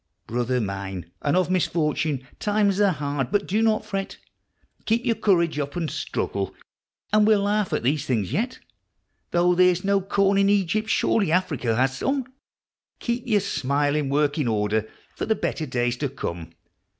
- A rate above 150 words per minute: Yes, average, 170 wpm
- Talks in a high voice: No, medium, 165 Hz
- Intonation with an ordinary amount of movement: No, wide, 7.6 semitones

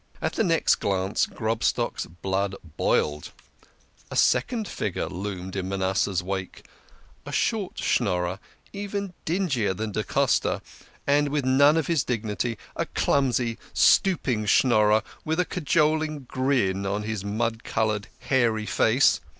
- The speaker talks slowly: Yes, slow, 130 wpm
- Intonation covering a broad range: Yes, wide, 6.7 semitones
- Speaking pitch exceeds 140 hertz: No, low, 115 Hz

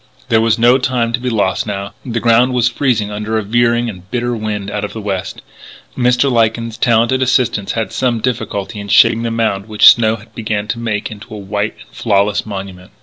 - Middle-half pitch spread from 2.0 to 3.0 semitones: Yes, narrow, 2.4 semitones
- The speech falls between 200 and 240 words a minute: Yes, fast, 205 wpm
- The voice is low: Yes, low, 110 Hz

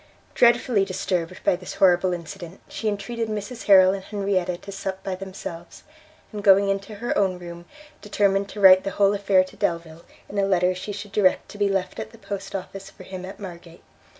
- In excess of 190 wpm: Yes, average, 200 wpm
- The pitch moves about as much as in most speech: No, narrow, 1.7 semitones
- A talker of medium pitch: No, high, 195 Hz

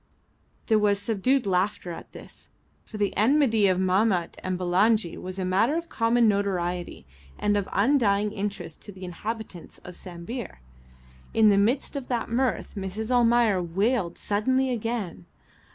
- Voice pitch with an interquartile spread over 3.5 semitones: Yes, average, 3.9 semitones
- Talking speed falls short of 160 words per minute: Yes, average, 150 wpm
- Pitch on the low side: No, high, 205 Hz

